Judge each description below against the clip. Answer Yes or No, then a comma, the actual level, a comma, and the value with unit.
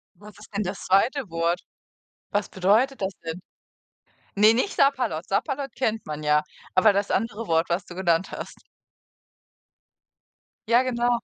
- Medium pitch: No, high, 205 Hz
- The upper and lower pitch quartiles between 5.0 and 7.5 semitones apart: Yes, average, 5.3 semitones